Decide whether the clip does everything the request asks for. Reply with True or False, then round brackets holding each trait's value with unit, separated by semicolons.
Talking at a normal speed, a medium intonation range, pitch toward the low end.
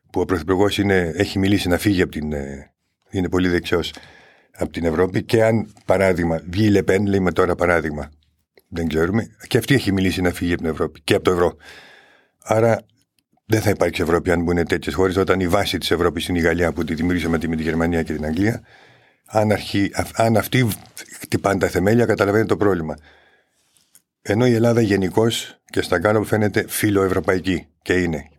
False (180 wpm; 3.9 semitones; 95 Hz)